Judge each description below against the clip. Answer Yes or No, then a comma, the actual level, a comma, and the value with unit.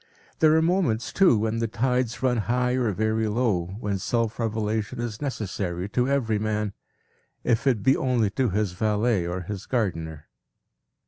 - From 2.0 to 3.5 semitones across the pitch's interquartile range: Yes, average, 3.2 semitones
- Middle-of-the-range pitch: No, low, 110 Hz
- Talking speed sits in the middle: Yes, average, 160 wpm